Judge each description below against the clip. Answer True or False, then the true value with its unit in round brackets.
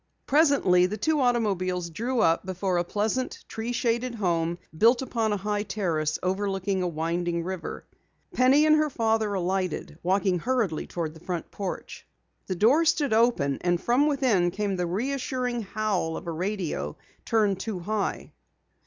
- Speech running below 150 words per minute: False (155 wpm)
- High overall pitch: True (200 Hz)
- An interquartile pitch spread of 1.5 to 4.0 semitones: False (5.1 semitones)